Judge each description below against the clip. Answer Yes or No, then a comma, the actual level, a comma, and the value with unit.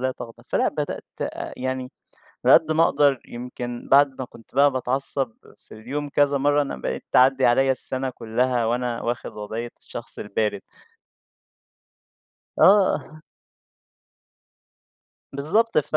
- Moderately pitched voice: No, low, 130 Hz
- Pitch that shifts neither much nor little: Yes, average, 3.0 semitones